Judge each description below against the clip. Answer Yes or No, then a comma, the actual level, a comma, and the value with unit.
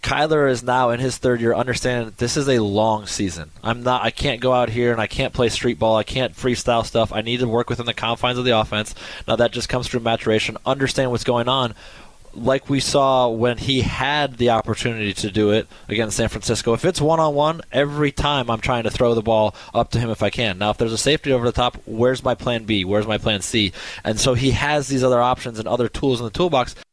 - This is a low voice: Yes, low, 120 Hz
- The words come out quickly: Yes, fast, 245 wpm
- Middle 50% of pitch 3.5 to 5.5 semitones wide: No, average, 2.8 semitones